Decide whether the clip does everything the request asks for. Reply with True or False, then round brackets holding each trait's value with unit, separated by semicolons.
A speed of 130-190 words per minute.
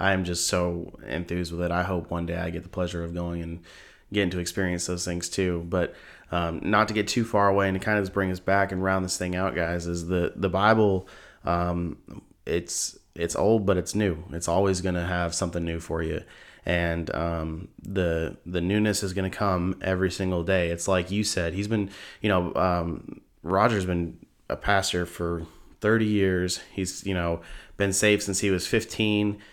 False (205 wpm)